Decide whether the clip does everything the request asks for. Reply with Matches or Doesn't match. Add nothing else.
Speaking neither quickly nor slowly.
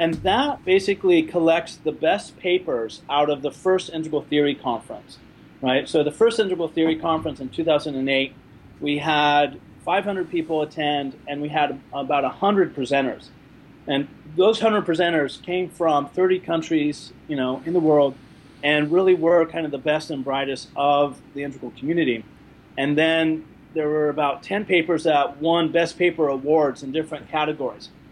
Matches